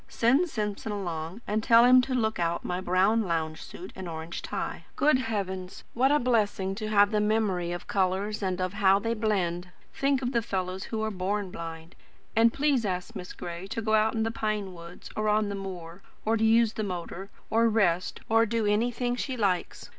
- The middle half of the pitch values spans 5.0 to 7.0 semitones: No, average, 3.7 semitones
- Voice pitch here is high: Yes, high, 210 Hz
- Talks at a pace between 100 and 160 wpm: No, average, 200 wpm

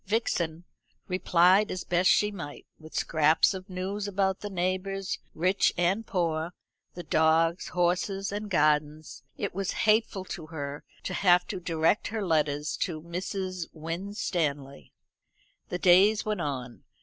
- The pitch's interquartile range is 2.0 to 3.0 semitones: No, average, 3.5 semitones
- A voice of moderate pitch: Yes, medium, 180 Hz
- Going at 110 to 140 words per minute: Yes, slow, 135 wpm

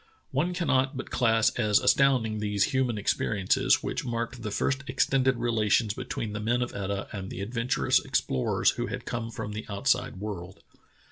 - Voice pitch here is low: Yes, low, 115 Hz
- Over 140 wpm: Yes, average, 165 wpm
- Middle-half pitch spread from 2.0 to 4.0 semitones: Yes, average, 3.5 semitones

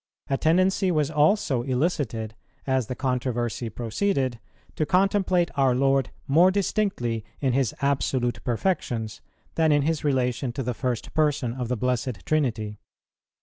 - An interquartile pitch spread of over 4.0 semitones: Yes, average, 4.4 semitones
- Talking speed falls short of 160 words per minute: Yes, average, 140 wpm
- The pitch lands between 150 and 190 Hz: No, low, 130 Hz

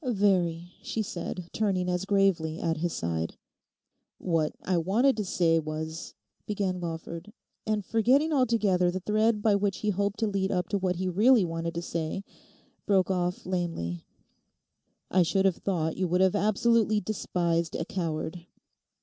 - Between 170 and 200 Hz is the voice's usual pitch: Yes, medium, 185 Hz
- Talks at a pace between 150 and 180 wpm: Yes, average, 160 wpm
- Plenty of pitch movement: No, average, 3.6 semitones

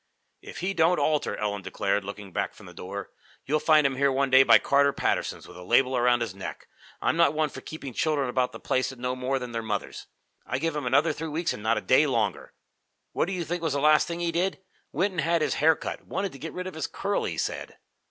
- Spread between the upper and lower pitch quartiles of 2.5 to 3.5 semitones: No, average, 4.8 semitones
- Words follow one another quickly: Yes, fast, 255 wpm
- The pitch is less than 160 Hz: Yes, medium, 140 Hz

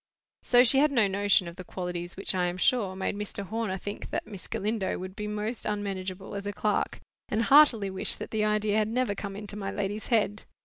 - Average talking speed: No, fast, 220 wpm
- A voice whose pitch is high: Yes, high, 205 Hz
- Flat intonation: Yes, narrow, 2.1 semitones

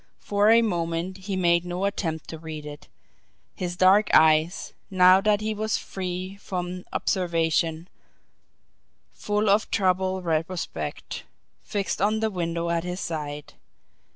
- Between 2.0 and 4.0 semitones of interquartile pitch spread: Yes, average, 3.0 semitones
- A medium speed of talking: No, slow, 130 wpm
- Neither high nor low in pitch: Yes, medium, 180 Hz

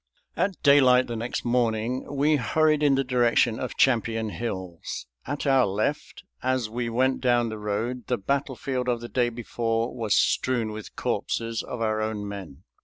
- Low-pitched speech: Yes, low, 120 Hz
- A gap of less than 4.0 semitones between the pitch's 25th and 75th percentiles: Yes, average, 2.7 semitones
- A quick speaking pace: No, average, 170 wpm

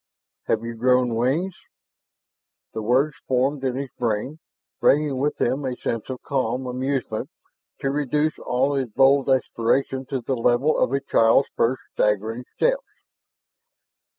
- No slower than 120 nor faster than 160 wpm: Yes, average, 140 wpm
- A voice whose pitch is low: Yes, low, 130 Hz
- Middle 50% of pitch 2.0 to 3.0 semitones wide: Yes, narrow, 2.4 semitones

